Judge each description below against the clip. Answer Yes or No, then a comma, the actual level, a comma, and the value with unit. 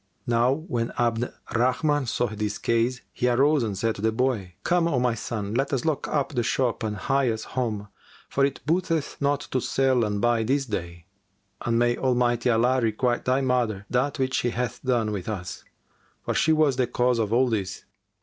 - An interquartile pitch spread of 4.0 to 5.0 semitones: No, average, 3.0 semitones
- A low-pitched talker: Yes, low, 120 Hz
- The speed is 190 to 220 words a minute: Yes, average, 200 wpm